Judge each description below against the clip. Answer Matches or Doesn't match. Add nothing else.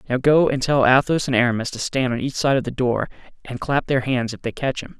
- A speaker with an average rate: Doesn't match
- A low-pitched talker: Matches